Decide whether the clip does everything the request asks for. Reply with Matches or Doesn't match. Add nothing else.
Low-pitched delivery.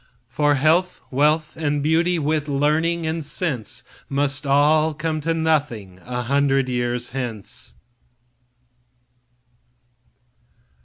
Doesn't match